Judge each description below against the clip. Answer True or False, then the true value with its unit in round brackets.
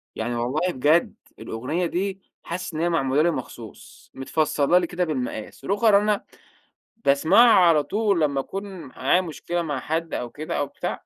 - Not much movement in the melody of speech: False (4.9 semitones)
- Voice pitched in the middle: True (165 Hz)